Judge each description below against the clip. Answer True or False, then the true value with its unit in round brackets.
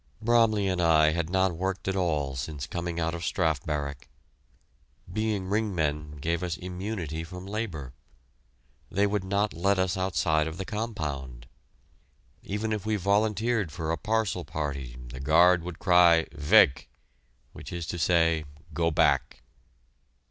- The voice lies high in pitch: False (85 Hz)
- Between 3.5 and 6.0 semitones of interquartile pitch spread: True (4.1 semitones)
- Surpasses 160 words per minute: False (150 wpm)